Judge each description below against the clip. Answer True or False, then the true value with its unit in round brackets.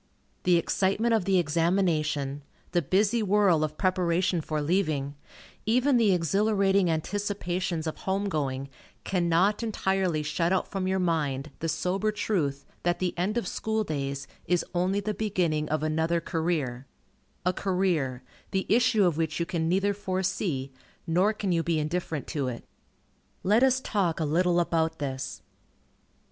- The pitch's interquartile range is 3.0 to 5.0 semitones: True (4.0 semitones)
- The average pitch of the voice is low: False (175 Hz)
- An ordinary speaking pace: True (150 wpm)